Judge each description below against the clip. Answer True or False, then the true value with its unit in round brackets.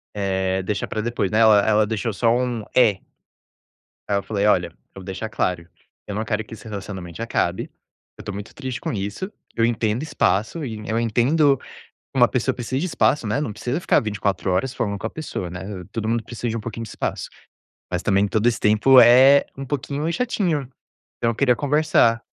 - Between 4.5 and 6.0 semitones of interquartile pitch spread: False (3.8 semitones)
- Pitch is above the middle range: False (110 Hz)